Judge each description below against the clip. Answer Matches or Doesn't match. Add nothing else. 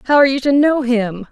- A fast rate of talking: Matches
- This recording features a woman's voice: Matches